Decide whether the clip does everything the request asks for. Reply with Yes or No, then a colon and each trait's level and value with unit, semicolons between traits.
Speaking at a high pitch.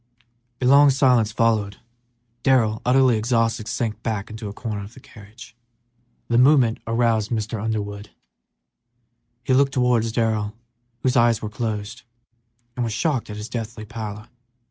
No: low, 115 Hz